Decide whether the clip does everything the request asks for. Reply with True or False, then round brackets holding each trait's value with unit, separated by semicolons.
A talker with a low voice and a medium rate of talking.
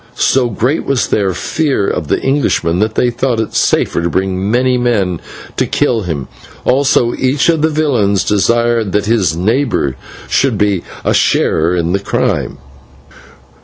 True (110 Hz; 160 wpm)